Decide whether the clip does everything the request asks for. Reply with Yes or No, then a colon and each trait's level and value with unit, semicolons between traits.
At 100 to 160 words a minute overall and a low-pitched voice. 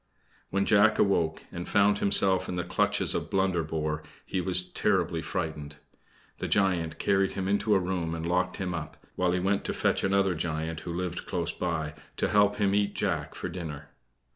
No: average, 185 wpm; very low, 90 Hz